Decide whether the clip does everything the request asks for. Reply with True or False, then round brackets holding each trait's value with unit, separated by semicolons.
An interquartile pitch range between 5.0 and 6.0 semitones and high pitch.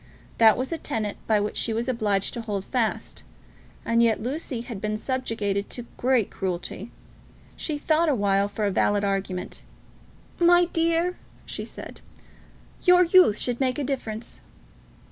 True (5.4 semitones; 230 Hz)